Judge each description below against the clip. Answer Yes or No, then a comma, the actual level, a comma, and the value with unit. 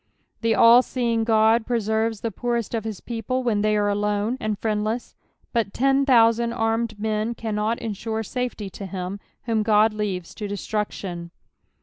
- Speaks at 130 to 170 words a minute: Yes, average, 160 wpm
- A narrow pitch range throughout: Yes, narrow, 1.9 semitones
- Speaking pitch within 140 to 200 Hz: No, high, 220 Hz